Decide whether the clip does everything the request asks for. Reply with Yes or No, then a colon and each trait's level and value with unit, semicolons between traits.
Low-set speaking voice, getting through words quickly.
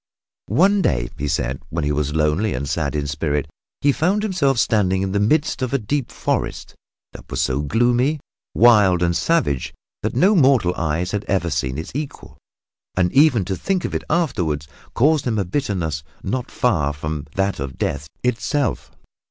No: very low, 95 Hz; average, 175 wpm